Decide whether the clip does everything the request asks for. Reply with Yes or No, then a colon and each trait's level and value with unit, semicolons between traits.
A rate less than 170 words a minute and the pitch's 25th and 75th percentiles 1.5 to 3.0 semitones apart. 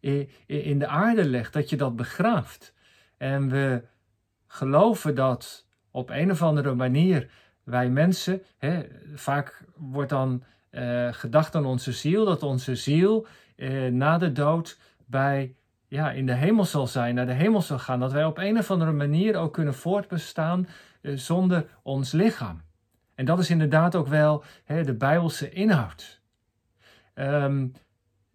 No: average, 150 wpm; average, 4.4 semitones